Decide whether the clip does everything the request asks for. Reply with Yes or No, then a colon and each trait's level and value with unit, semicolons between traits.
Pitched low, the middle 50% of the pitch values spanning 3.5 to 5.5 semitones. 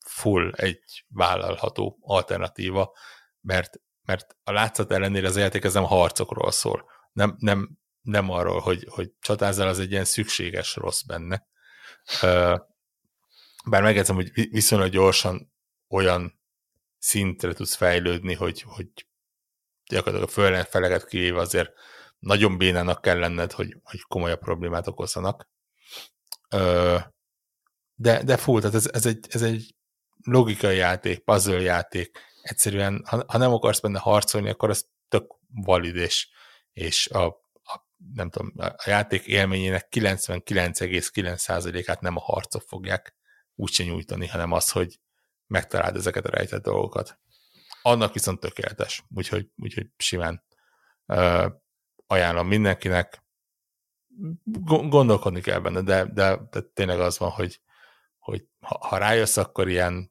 No: very low, 95 Hz; average, 3.0 semitones